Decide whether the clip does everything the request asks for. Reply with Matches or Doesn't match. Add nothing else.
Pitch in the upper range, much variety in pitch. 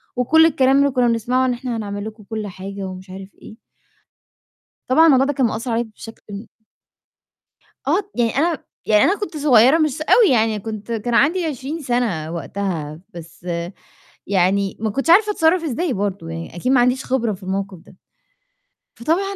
Matches